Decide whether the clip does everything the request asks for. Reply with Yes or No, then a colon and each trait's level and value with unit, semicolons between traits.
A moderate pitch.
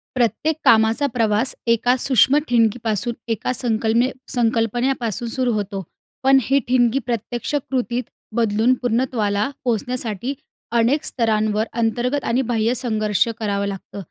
No: high, 235 Hz